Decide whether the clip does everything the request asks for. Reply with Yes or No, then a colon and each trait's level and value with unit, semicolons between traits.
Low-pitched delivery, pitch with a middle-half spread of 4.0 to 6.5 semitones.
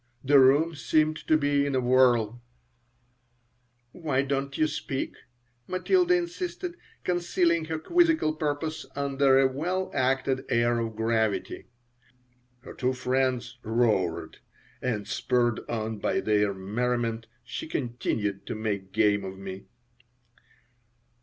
Yes: low, 130 Hz; wide, 5.4 semitones